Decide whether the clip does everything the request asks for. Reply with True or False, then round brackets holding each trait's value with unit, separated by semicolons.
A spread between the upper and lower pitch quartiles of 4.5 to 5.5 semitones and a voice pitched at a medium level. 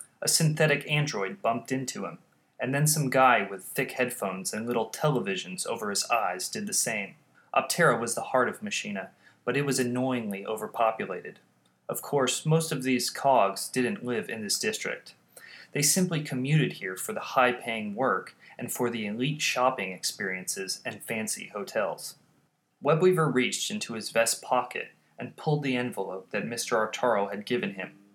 False (5.2 semitones; 130 Hz)